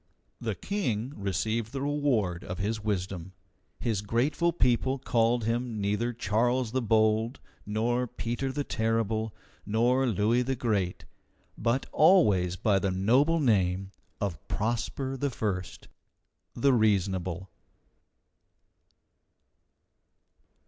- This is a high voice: No, low, 115 Hz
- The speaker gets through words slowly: Yes, slow, 105 wpm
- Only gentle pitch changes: No, average, 3.8 semitones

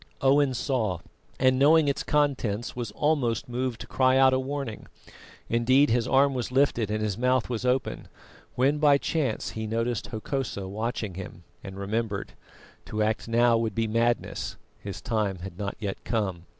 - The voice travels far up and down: No, average, 3.6 semitones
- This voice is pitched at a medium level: No, low, 120 Hz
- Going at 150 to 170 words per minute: Yes, average, 165 wpm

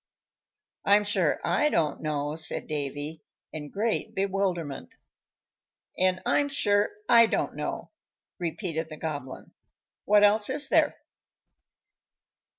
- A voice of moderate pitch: Yes, medium, 180 Hz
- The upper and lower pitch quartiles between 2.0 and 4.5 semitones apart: No, average, 5.2 semitones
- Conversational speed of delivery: No, slow, 110 wpm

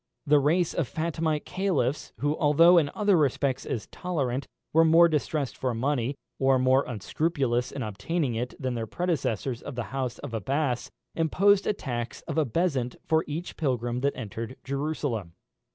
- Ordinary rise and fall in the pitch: Yes, average, 4.5 semitones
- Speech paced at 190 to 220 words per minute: No, average, 165 wpm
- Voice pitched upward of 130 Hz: Yes, medium, 140 Hz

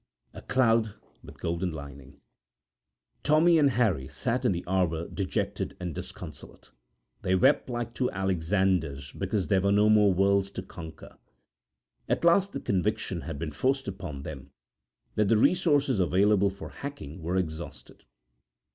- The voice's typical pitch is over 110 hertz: No, very low, 95 Hz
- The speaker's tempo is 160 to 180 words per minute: No, average, 145 wpm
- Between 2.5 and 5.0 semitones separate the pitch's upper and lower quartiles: No, wide, 5.4 semitones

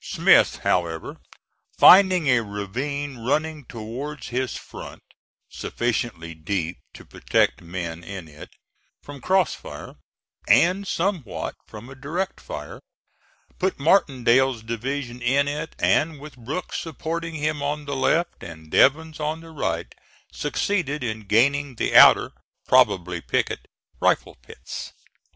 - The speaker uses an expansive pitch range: Yes, wide, 5.9 semitones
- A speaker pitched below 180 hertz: Yes, low, 135 Hz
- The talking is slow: Yes, slow, 125 wpm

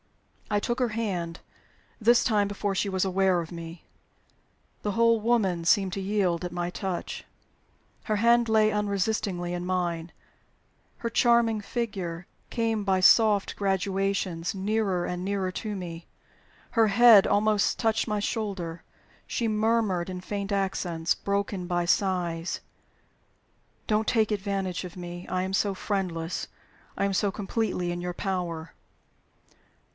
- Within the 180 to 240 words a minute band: No, average, 140 wpm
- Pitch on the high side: Yes, high, 195 Hz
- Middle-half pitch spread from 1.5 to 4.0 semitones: Yes, average, 3.2 semitones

